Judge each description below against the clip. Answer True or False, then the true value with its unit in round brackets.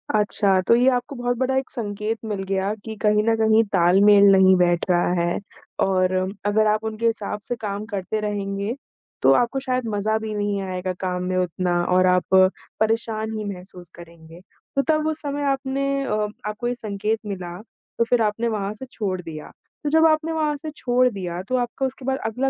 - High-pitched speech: True (215 Hz)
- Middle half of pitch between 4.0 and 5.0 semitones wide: True (4.4 semitones)